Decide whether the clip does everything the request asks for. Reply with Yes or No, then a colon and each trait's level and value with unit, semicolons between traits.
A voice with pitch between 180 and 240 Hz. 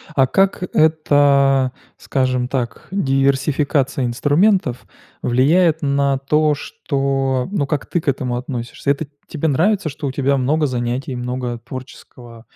No: low, 135 Hz